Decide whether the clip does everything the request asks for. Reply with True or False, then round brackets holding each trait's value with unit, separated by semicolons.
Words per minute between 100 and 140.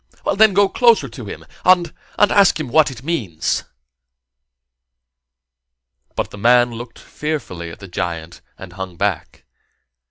True (135 wpm)